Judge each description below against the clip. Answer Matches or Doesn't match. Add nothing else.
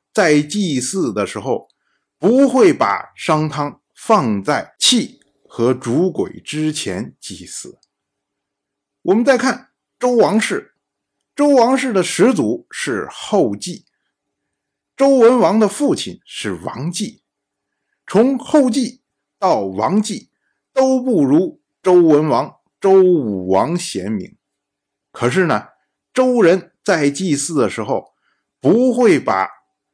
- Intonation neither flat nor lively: Doesn't match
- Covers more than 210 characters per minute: Doesn't match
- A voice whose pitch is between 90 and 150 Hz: Doesn't match